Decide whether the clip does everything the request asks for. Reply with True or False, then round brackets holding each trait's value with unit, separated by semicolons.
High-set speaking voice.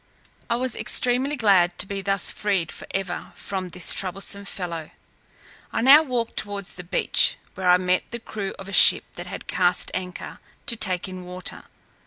True (195 Hz)